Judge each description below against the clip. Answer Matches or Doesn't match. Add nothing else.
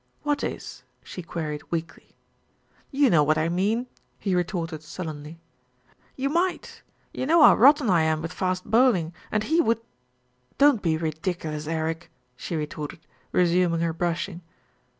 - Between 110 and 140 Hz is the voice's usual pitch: Doesn't match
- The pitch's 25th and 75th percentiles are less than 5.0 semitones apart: Doesn't match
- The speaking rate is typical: Matches